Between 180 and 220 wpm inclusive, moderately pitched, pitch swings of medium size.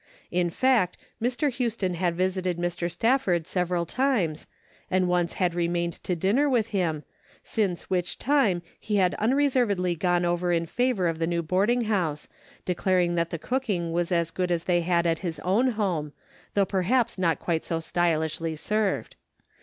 No: average, 165 wpm; medium, 180 Hz; average, 3.7 semitones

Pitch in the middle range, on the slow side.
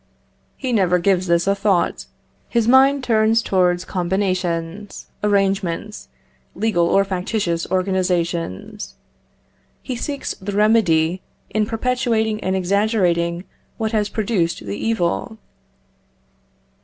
No: high, 195 Hz; slow, 105 wpm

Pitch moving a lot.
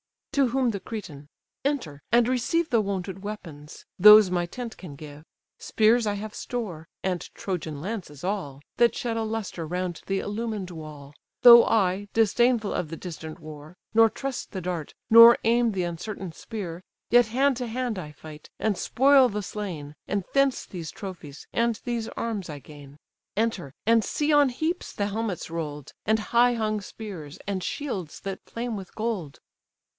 Yes: wide, 5.7 semitones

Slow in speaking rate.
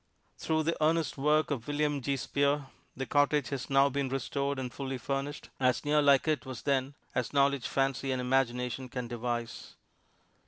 No: average, 170 wpm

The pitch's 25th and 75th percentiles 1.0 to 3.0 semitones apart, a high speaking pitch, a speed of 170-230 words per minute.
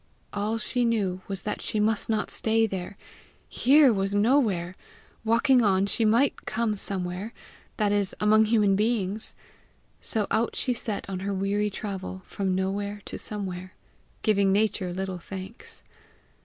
No: narrow, 2.4 semitones; high, 205 Hz; average, 150 wpm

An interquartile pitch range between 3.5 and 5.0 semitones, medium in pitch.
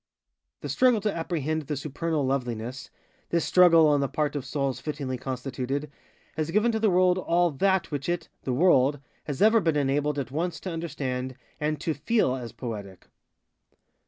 Yes: average, 4.4 semitones; medium, 150 Hz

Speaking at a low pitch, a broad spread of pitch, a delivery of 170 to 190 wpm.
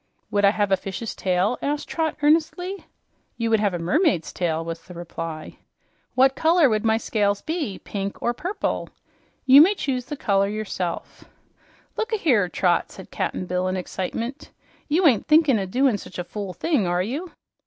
No: high, 215 Hz; wide, 8.1 semitones; average, 175 wpm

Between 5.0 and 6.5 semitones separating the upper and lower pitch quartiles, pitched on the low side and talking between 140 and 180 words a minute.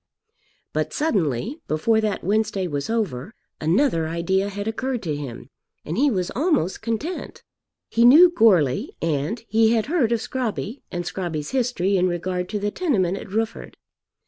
No: average, 5.3 semitones; high, 205 Hz; average, 155 wpm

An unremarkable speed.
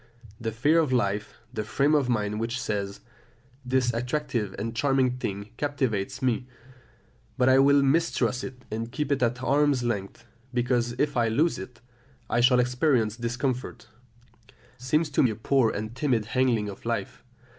Yes: average, 160 wpm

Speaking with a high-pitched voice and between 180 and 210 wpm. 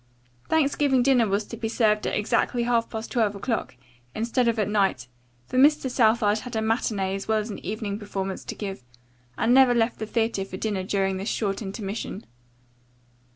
Yes: high, 220 Hz; average, 185 wpm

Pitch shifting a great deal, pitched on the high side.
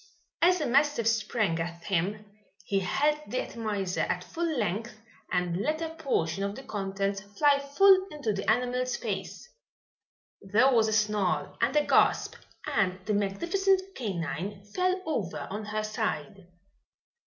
Yes: wide, 6.4 semitones; high, 215 Hz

